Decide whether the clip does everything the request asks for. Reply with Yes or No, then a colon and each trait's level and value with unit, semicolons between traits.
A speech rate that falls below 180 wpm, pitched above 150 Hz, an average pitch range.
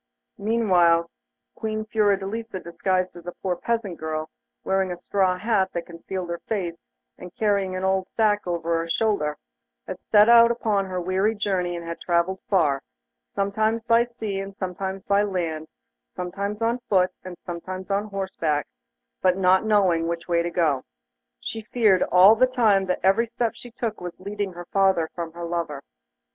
Yes: average, 170 wpm; high, 190 Hz; average, 3.3 semitones